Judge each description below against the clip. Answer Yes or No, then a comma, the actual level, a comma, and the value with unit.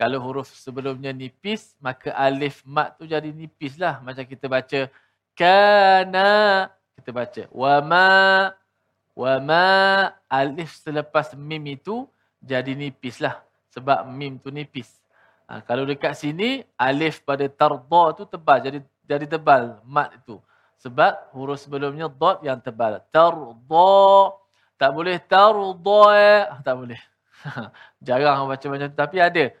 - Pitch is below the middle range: No, medium, 150 Hz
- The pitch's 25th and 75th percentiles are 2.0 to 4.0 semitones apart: No, average, 5.3 semitones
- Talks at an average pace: No, fast, 130 wpm